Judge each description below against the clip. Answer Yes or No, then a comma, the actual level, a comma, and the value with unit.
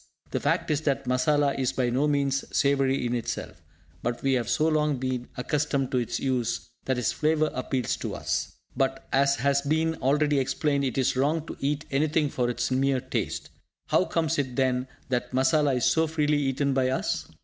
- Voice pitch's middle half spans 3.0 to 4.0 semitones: No, narrow, 2.5 semitones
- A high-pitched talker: No, low, 135 Hz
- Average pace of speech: Yes, average, 195 wpm